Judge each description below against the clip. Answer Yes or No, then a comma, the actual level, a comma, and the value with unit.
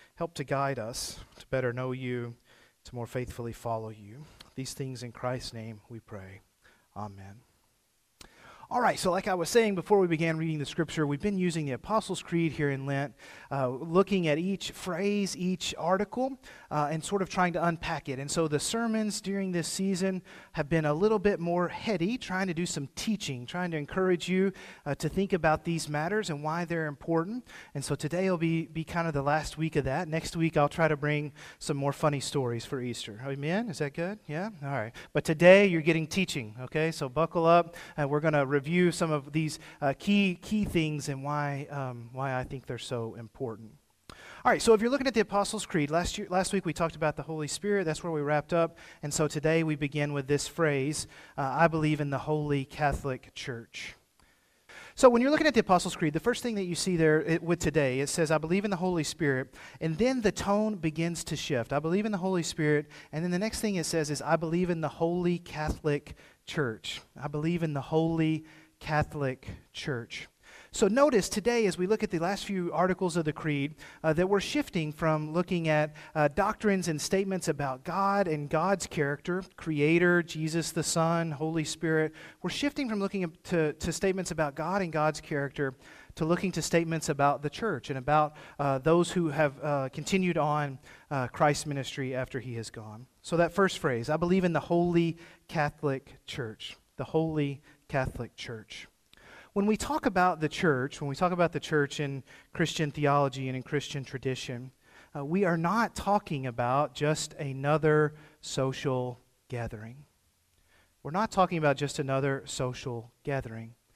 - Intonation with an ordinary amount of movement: Yes, average, 4.1 semitones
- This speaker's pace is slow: No, average, 200 wpm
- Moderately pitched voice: Yes, medium, 155 Hz